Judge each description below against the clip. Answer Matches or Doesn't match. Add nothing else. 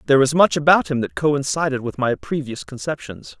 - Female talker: Doesn't match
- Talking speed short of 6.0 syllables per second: Matches